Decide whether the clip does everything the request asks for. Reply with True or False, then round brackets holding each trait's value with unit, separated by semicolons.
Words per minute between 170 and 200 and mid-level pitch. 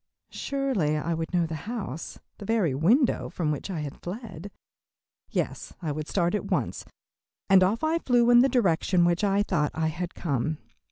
True (180 wpm; 180 Hz)